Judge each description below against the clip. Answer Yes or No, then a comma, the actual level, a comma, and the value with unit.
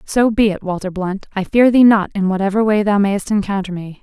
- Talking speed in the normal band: No, fast, 240 wpm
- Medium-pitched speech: No, high, 200 Hz